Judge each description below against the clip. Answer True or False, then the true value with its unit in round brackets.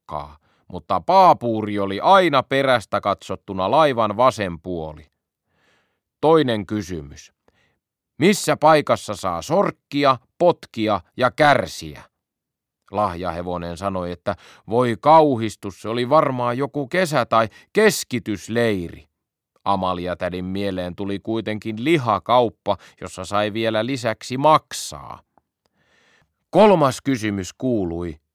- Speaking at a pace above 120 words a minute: False (95 wpm)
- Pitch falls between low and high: False (110 Hz)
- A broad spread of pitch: True (6.6 semitones)